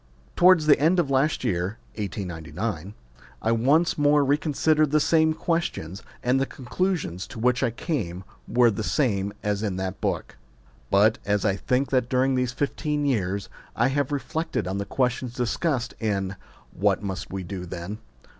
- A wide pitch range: Yes, wide, 6.5 semitones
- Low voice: Yes, low, 120 Hz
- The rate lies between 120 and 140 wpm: No, average, 165 wpm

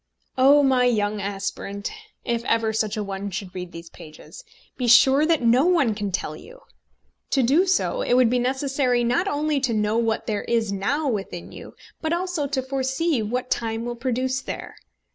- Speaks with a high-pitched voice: Yes, high, 245 Hz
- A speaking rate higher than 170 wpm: Yes, average, 185 wpm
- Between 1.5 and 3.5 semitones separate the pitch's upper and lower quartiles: No, average, 4.6 semitones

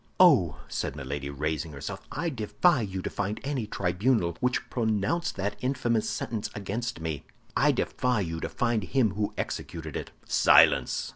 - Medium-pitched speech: No, low, 105 Hz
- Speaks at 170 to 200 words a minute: No, average, 155 wpm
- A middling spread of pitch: No, wide, 6.8 semitones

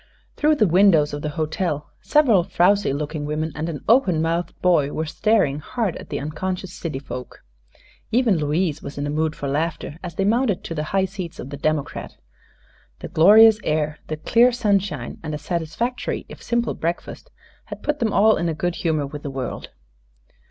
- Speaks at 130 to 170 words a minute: No, average, 185 wpm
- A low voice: No, medium, 165 Hz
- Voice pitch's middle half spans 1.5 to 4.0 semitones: No, average, 5.1 semitones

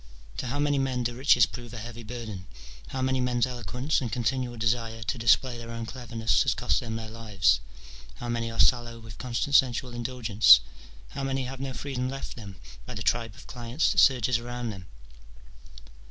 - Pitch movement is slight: Yes, narrow, 2.1 semitones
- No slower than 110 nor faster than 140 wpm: No, average, 195 wpm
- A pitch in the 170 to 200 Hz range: No, low, 120 Hz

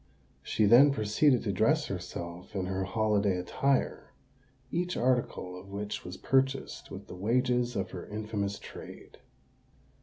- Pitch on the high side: No, low, 105 Hz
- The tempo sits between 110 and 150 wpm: Yes, average, 140 wpm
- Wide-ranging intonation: No, average, 4.7 semitones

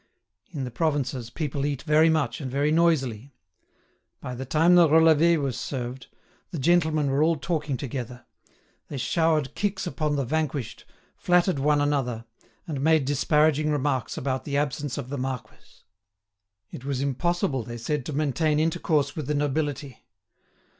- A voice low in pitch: No, medium, 145 Hz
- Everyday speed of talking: Yes, average, 155 wpm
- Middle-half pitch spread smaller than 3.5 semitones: Yes, average, 3.0 semitones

